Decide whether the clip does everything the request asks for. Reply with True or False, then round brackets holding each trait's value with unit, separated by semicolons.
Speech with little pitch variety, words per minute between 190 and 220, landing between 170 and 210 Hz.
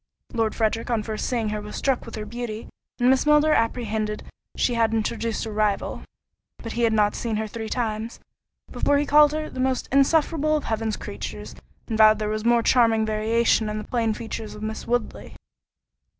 False (2.3 semitones; 195 wpm; 225 Hz)